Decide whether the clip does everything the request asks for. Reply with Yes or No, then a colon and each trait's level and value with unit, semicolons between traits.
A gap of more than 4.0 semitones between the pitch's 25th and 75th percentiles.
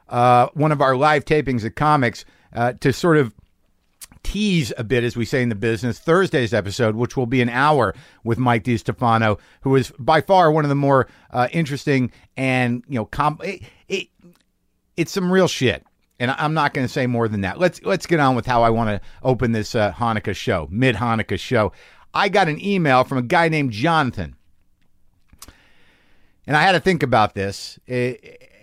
Yes: average, 5.0 semitones